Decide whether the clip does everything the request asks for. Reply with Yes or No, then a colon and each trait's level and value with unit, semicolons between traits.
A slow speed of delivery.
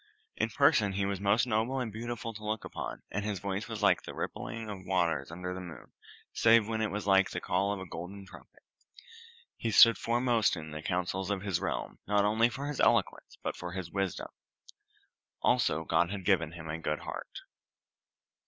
No: average, 195 wpm